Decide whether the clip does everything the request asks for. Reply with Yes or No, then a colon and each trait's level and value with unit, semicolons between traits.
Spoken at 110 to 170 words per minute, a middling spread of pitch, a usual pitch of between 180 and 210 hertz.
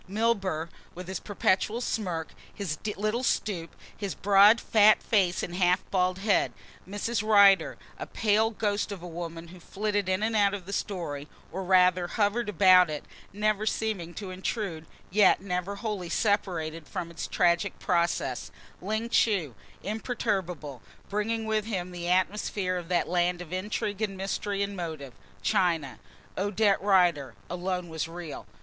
Yes: average, 150 wpm; average, 3.0 semitones; high, 190 Hz